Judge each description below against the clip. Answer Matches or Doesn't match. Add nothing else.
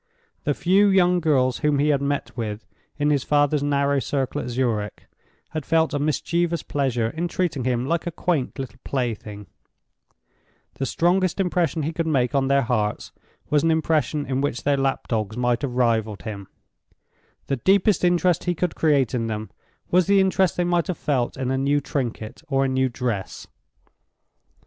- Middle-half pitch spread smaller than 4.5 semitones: Doesn't match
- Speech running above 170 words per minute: Matches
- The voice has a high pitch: Doesn't match